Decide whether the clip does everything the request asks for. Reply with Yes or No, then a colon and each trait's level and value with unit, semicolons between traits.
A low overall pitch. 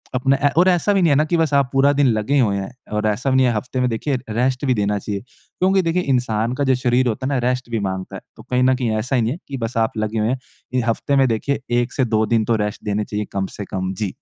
Yes: low, 125 Hz